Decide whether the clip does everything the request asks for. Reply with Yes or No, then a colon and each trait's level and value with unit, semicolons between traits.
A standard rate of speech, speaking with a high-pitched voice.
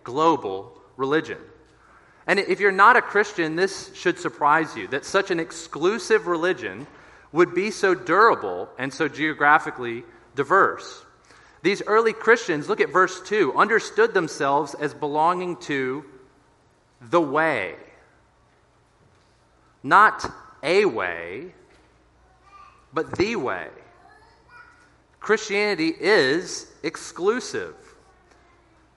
No: slow, 100 wpm; high, 195 Hz